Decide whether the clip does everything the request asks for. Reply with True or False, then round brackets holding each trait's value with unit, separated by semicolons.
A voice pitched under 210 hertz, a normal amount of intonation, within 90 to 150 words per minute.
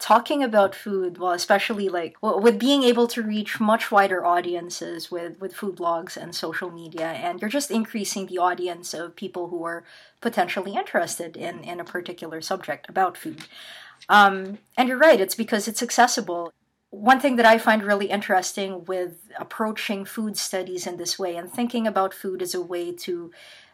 False (190 Hz; 4.1 semitones; 180 wpm)